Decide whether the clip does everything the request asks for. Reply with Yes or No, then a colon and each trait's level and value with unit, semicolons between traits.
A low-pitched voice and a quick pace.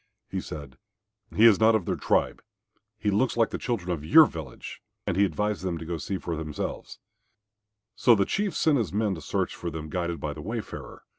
Yes: very low, 95 Hz; fast, 220 wpm